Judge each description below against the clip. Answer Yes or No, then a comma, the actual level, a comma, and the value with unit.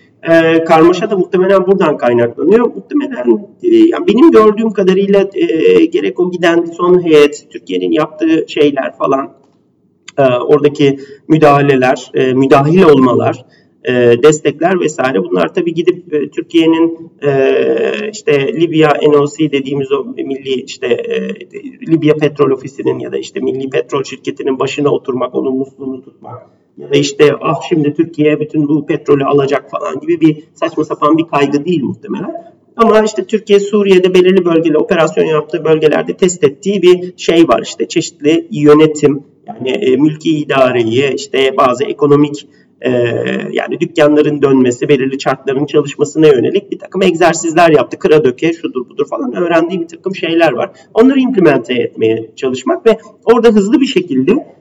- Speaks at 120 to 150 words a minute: Yes, fast, 140 wpm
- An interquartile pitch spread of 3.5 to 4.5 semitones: No, average, 5.1 semitones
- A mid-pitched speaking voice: Yes, medium, 160 Hz